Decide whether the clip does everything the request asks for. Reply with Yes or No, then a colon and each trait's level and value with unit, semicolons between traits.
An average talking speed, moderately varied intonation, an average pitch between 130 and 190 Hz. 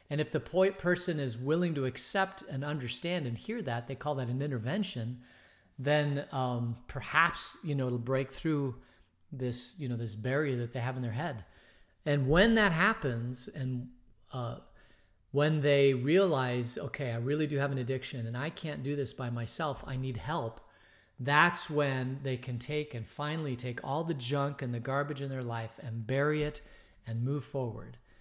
Yes: average, 185 wpm; average, 3.5 semitones; low, 135 Hz